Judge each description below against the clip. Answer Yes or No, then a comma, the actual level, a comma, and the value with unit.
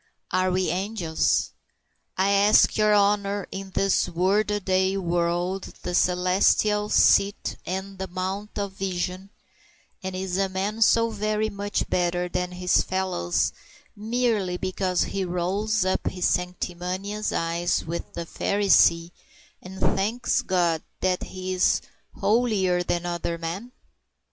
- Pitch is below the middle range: No, high, 190 Hz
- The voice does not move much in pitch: Yes, narrow, 2.2 semitones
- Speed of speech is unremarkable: No, slow, 130 wpm